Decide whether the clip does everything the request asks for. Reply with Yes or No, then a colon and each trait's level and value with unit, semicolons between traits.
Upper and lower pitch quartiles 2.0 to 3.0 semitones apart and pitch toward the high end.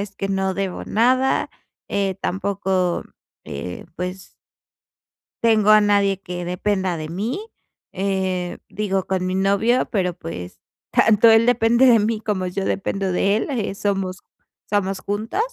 Yes: narrow, 2.4 semitones; high, 195 Hz